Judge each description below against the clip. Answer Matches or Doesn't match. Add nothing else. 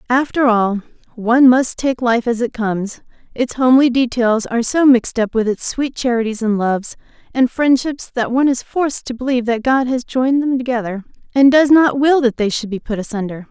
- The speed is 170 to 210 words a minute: Matches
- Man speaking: Doesn't match